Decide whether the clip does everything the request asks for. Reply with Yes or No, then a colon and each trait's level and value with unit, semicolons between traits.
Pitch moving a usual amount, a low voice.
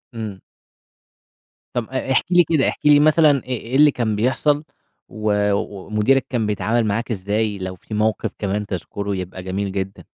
Yes: average, 4.4 semitones; low, 105 Hz